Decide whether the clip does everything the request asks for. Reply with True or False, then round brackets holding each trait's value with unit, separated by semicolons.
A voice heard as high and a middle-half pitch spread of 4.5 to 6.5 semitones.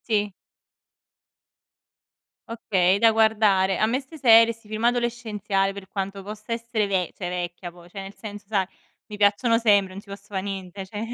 False (205 Hz; 2.6 semitones)